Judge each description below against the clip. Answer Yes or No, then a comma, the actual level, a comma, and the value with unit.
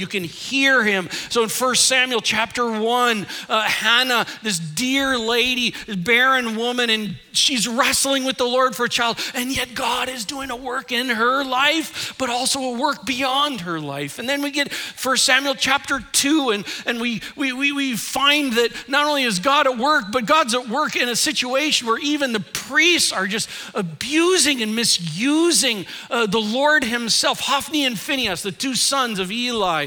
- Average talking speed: Yes, average, 190 wpm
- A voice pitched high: Yes, very high, 250 Hz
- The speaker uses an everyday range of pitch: Yes, average, 3.4 semitones